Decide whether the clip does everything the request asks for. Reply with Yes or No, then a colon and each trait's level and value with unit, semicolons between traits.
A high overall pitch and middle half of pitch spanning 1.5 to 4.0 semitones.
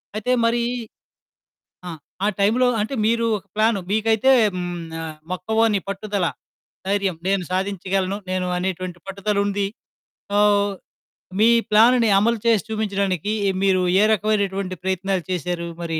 Yes: high, 200 Hz; narrow, 2.6 semitones